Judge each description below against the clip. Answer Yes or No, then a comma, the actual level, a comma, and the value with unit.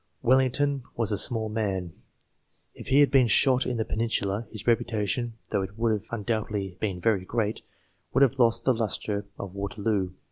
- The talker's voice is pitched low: Yes, low, 110 Hz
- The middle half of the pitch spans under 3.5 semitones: Yes, average, 2.9 semitones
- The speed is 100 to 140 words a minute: No, average, 175 wpm